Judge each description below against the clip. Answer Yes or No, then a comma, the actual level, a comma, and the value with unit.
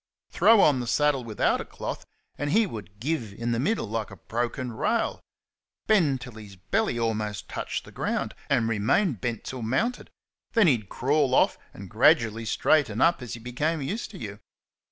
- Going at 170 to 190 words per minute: Yes, average, 180 wpm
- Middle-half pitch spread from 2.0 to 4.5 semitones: No, wide, 5.4 semitones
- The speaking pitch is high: No, low, 125 Hz